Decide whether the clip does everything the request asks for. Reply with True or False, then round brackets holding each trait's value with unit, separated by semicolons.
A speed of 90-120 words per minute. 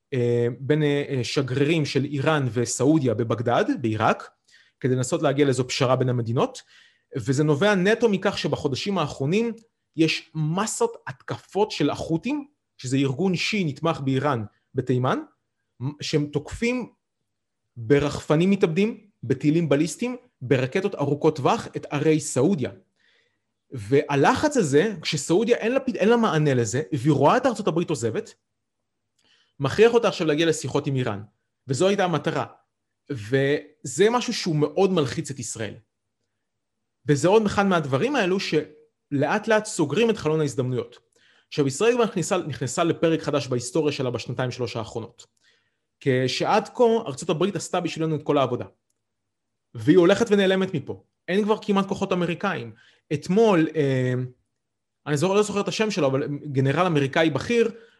False (130 wpm)